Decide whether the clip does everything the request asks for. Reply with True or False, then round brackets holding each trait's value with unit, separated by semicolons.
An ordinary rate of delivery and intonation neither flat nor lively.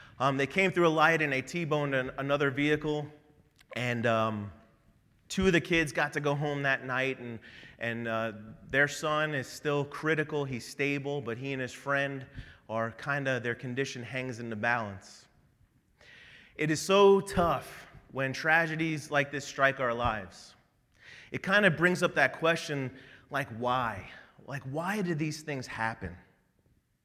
True (165 wpm; 4.0 semitones)